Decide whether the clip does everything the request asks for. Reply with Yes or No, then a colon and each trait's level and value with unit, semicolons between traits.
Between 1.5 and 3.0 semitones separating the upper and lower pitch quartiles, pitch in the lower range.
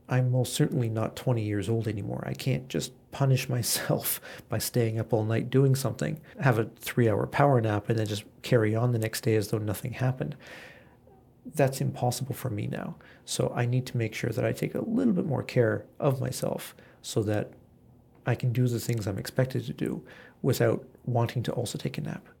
Yes: narrow, 2.6 semitones; low, 120 Hz